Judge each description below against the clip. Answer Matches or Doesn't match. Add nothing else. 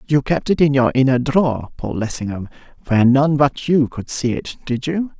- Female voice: Doesn't match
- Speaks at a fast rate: Doesn't match